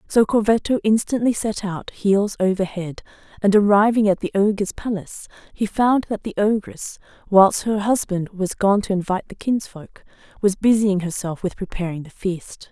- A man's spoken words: No, female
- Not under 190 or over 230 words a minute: No, average, 165 wpm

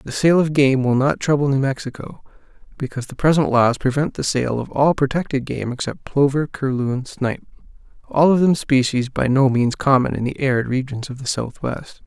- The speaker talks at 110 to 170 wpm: No, average, 195 wpm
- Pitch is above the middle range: No, low, 135 Hz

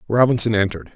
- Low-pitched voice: Yes, low, 110 Hz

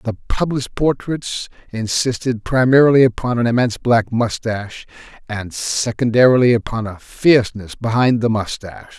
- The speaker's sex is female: No, male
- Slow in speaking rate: Yes, slow, 120 wpm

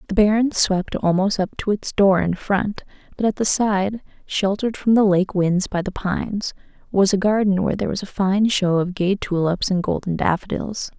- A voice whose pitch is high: Yes, high, 195 Hz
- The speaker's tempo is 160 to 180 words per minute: No, average, 200 wpm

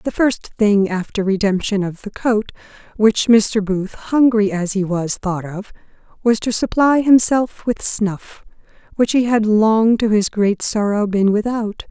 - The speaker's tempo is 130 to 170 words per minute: Yes, average, 165 wpm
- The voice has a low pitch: No, high, 210 Hz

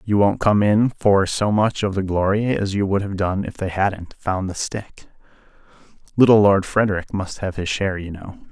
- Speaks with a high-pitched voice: No, low, 100 Hz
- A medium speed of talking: No, fast, 210 wpm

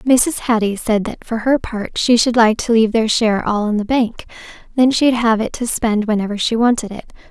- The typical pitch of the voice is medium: No, high, 225 Hz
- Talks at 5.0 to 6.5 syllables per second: Yes, 5.2 syllables/s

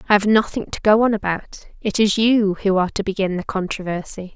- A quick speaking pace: Yes, fast, 220 wpm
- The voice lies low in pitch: No, high, 200 Hz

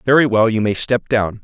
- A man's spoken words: Yes, male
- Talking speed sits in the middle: No, fast, 250 wpm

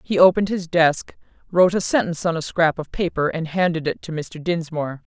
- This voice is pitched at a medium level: Yes, medium, 165 Hz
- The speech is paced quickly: Yes, fast, 210 wpm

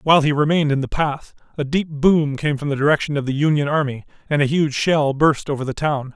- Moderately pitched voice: Yes, medium, 145 Hz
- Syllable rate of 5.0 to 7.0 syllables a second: Yes, 5.9 syllables/s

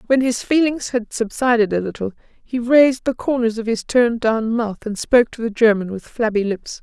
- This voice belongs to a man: No, female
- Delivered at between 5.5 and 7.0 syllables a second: No, 5.3 syllables/s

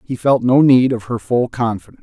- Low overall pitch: Yes, low, 120 Hz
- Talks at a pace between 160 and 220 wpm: No, fast, 235 wpm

